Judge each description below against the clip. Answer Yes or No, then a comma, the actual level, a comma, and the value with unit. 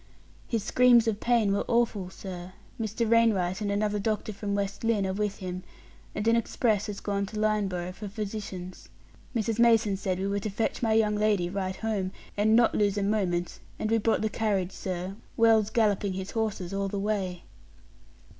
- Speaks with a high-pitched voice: Yes, high, 205 Hz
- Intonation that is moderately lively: No, narrow, 2.3 semitones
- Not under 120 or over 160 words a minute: No, average, 185 wpm